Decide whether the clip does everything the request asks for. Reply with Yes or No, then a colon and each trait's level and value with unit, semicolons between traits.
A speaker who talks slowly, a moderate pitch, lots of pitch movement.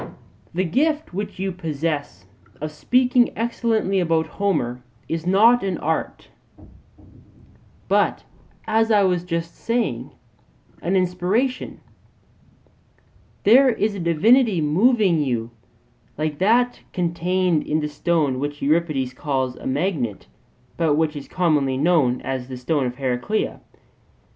Yes: slow, 120 wpm; medium, 170 Hz; wide, 5.7 semitones